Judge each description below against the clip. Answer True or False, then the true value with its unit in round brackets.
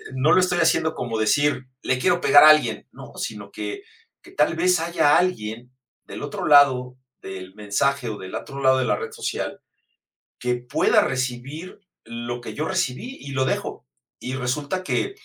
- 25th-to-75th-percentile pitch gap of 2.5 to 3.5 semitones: False (5.5 semitones)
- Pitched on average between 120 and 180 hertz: True (140 Hz)